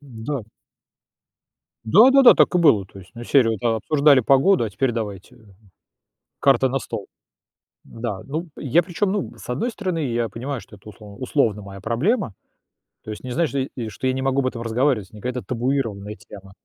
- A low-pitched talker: Yes, low, 125 Hz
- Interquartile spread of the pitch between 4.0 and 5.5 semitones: Yes, average, 4.6 semitones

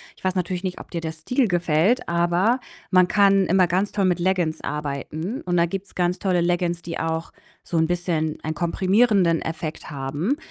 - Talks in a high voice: No, medium, 175 Hz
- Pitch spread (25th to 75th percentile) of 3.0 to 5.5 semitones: No, narrow, 2.6 semitones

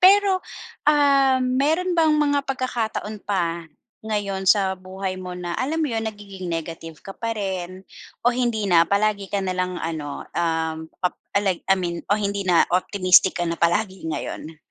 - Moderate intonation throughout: Yes, average, 5.0 semitones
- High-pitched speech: Yes, high, 195 Hz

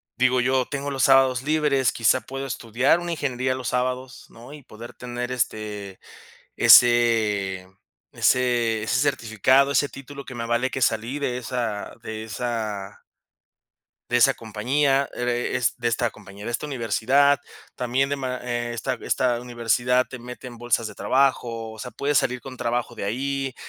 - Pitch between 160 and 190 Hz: No, low, 125 Hz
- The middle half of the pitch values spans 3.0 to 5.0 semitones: No, narrow, 2.4 semitones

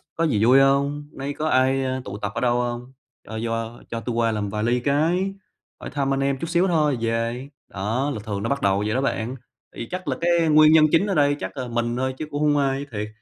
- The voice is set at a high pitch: No, low, 135 Hz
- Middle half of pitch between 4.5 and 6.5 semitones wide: No, average, 4.1 semitones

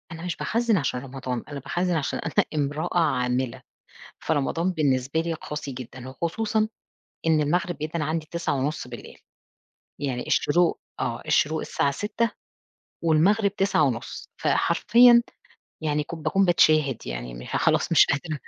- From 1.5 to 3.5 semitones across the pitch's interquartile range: No, average, 4.2 semitones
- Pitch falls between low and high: Yes, medium, 155 Hz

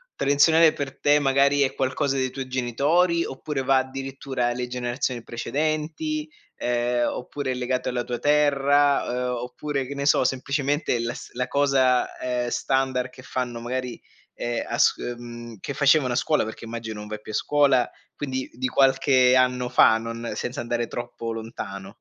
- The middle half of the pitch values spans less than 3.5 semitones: Yes, narrow, 2.6 semitones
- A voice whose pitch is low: Yes, low, 130 Hz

